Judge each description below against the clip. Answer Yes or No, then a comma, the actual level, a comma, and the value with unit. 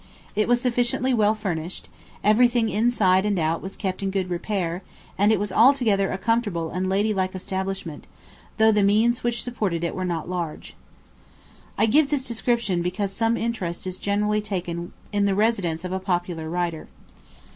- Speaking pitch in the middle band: No, high, 200 Hz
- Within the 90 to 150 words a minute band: No, average, 170 wpm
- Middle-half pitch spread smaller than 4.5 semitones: Yes, average, 3.7 semitones